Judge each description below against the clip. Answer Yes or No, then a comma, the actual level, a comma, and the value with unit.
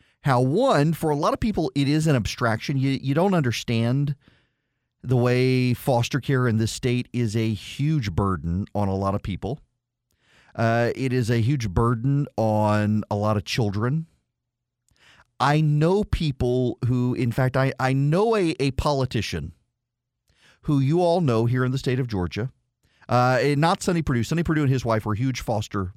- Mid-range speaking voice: No, low, 125 Hz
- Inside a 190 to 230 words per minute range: No, average, 180 wpm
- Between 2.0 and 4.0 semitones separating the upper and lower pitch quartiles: Yes, average, 3.6 semitones